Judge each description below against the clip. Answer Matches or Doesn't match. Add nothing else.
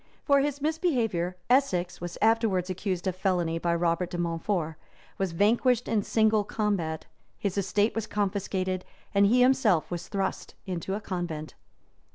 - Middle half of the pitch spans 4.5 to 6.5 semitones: Doesn't match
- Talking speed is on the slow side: Doesn't match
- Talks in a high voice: Matches